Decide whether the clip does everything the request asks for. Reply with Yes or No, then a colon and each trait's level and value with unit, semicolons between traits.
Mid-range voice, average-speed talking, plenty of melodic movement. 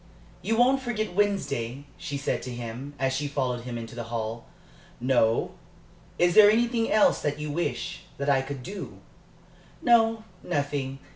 Yes: medium, 145 Hz; average, 155 wpm; wide, 8.7 semitones